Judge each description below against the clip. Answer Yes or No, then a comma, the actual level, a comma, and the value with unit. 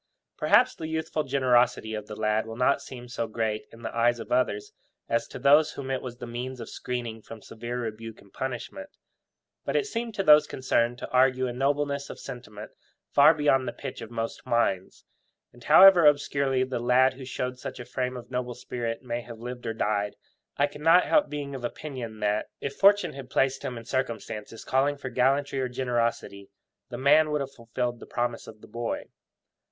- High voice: No, low, 125 Hz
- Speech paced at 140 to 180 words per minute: No, average, 200 wpm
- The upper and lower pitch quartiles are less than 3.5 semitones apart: Yes, average, 3.0 semitones